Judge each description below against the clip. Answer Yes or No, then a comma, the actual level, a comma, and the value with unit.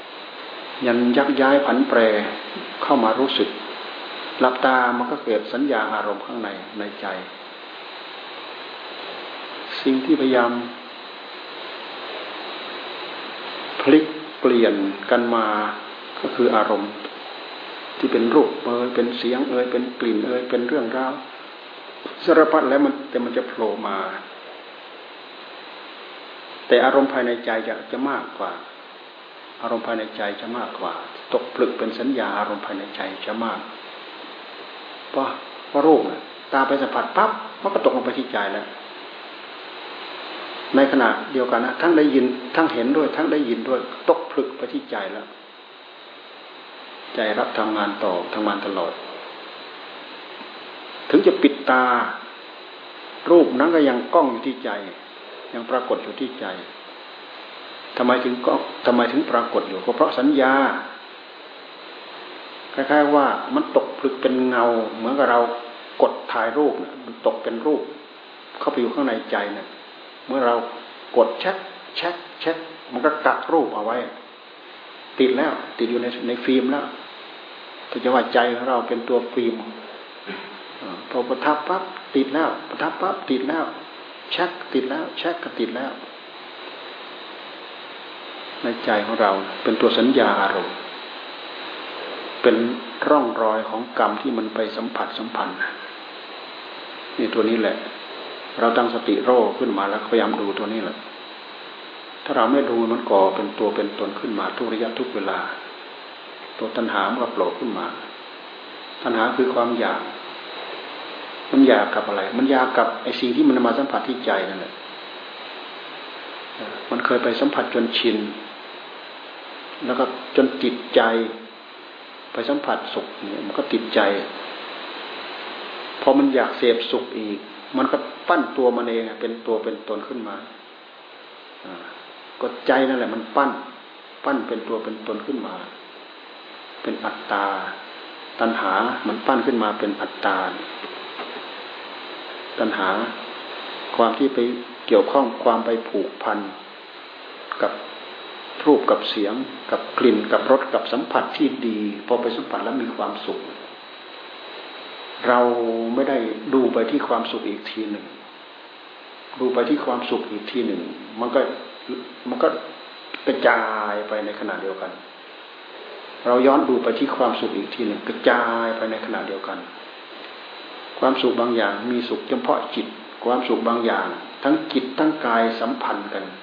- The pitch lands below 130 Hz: Yes, low, 120 Hz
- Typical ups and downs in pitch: No, narrow, 2.3 semitones